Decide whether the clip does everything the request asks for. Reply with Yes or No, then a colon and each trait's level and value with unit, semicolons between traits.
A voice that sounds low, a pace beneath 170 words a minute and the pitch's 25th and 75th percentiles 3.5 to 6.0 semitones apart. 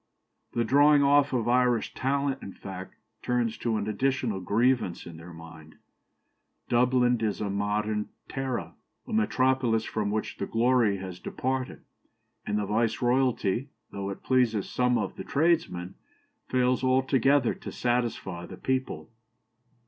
Yes: low, 120 Hz; slow, 135 wpm; average, 4.2 semitones